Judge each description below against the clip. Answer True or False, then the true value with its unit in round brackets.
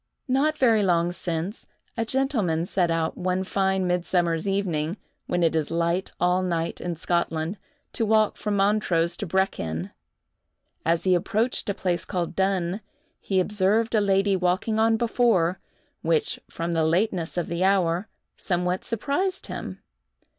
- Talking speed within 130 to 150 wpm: True (145 wpm)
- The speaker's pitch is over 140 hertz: True (185 Hz)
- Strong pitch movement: False (3.6 semitones)